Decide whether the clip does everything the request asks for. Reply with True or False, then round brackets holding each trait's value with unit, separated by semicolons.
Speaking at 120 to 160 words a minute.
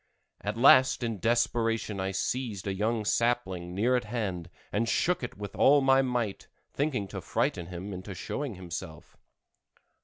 True (155 wpm)